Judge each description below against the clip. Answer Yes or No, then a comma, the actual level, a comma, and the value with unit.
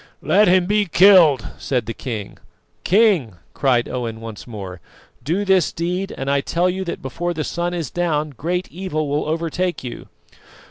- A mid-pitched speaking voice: Yes, medium, 165 Hz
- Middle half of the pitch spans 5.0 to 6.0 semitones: Yes, wide, 5.6 semitones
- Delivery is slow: No, average, 170 wpm